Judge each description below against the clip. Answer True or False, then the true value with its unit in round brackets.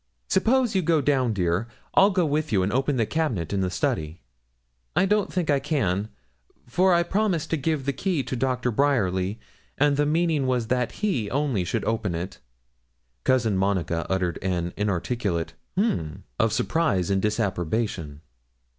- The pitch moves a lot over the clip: True (8.4 semitones)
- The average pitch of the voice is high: False (120 Hz)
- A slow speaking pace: False (165 wpm)